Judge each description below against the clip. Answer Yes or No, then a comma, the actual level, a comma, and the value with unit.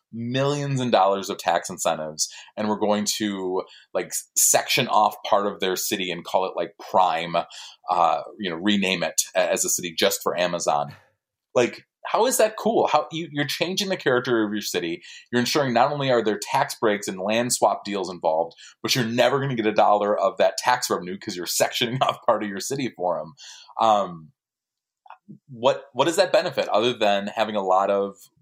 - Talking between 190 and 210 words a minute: Yes, average, 200 wpm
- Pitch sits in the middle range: No, low, 110 Hz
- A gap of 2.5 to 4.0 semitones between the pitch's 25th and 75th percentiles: No, average, 4.9 semitones